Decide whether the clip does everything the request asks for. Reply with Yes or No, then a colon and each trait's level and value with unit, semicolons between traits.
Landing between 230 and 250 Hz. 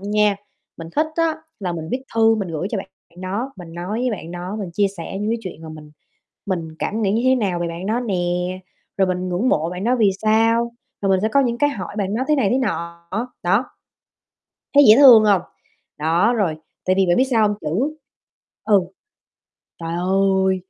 No: high, 195 Hz